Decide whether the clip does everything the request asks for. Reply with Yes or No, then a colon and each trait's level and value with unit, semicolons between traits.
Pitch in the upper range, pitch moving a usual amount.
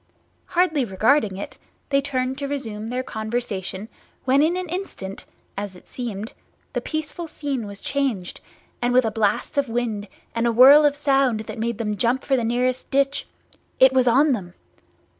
Yes: very high, 250 Hz; average, 4.3 semitones